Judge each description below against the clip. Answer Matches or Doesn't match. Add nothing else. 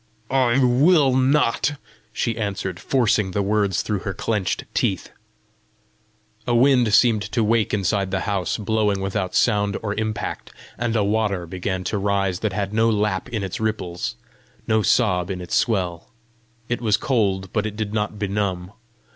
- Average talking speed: Matches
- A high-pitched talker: Doesn't match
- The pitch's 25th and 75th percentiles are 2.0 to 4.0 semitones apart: Matches